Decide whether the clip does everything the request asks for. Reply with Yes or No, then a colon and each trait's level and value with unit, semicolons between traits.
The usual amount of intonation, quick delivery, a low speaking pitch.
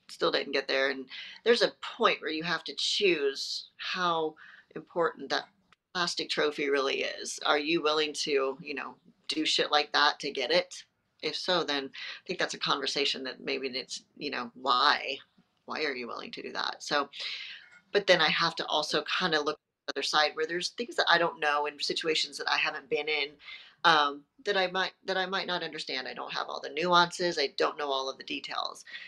No: average, 4.0 semitones; fast, 215 wpm; medium, 155 Hz